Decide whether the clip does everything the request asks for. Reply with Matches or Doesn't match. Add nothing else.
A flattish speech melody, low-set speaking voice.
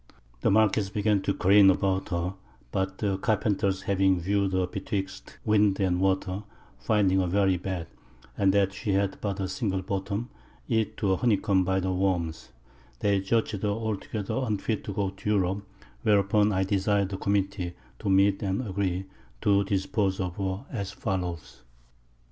Matches